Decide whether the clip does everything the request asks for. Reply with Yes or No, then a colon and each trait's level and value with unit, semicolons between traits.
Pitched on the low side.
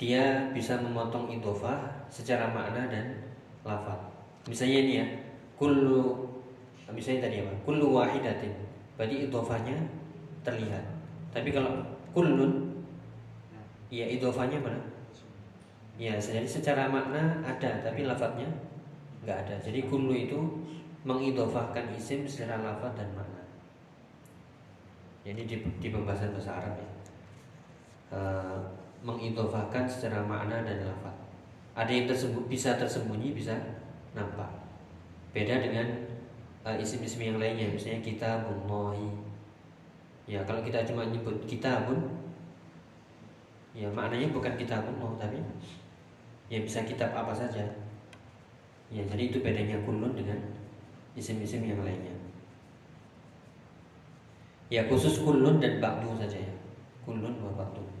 Yes: low, 115 Hz